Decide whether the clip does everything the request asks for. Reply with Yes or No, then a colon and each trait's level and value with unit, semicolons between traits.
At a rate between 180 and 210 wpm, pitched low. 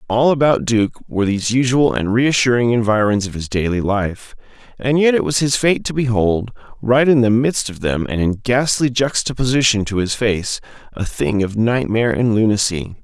Yes: average, 185 wpm; low, 115 Hz